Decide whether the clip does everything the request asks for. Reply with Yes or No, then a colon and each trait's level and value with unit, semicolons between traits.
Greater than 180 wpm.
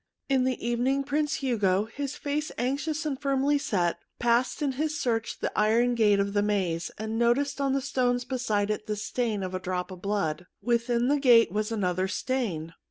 Yes: average, 190 wpm